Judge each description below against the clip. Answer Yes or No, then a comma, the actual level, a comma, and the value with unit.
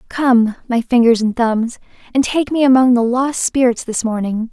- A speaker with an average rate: Yes, average, 185 wpm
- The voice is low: No, high, 245 Hz